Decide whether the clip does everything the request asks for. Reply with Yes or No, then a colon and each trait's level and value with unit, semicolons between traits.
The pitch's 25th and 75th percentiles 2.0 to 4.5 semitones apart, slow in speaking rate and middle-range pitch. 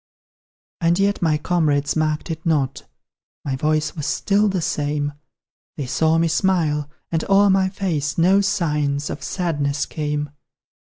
No: average, 3.3 semitones; average, 145 wpm; medium, 155 Hz